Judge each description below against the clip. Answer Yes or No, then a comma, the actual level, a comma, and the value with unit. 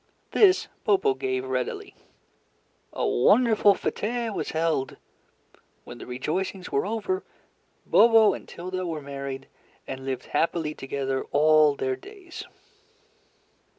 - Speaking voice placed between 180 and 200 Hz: Yes, medium, 185 Hz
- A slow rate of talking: Yes, slow, 115 wpm